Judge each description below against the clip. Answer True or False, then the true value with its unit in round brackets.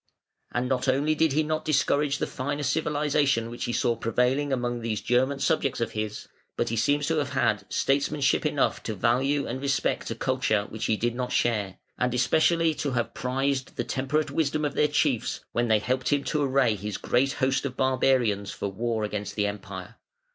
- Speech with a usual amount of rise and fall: True (3.7 semitones)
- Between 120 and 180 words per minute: False (195 wpm)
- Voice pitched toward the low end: True (130 Hz)